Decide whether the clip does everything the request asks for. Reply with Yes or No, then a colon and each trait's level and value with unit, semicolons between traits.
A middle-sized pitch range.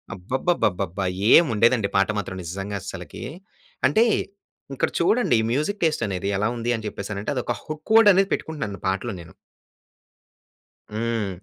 No: wide, 7.6 semitones